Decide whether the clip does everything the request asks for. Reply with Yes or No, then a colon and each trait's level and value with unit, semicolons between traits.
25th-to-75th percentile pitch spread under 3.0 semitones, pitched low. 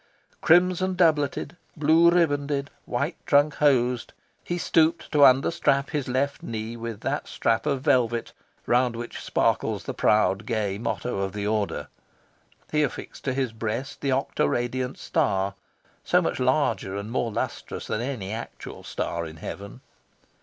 No: average, 4.6 semitones; low, 130 Hz